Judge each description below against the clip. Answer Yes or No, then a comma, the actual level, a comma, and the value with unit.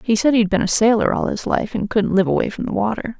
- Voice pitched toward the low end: No, high, 215 Hz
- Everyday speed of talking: No, fast, 300 wpm